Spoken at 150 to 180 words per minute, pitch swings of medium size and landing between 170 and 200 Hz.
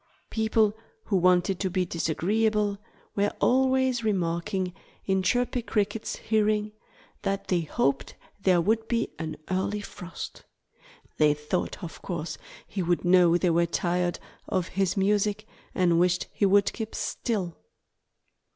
No: slow, 135 wpm; average, 3.4 semitones; high, 190 Hz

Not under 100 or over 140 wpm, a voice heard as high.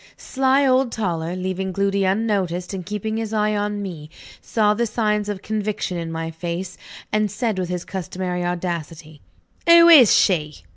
No: average, 160 wpm; high, 195 Hz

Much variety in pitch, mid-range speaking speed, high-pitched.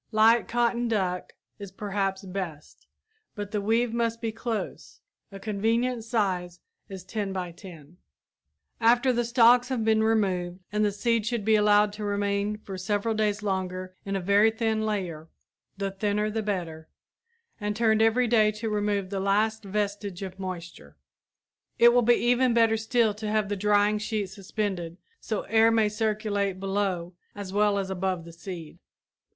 No: narrow, 2.5 semitones; average, 165 wpm; high, 205 Hz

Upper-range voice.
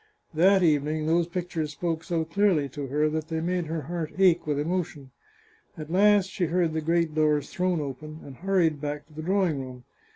No: medium, 160 Hz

